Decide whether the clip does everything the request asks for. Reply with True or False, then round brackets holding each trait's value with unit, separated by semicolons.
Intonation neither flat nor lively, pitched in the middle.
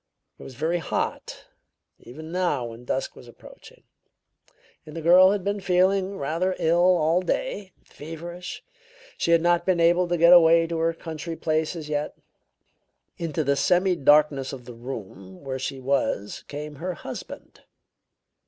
True (3.9 semitones; 165 Hz)